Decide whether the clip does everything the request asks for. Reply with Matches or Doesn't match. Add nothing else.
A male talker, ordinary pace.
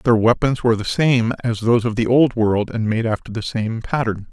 Doesn't match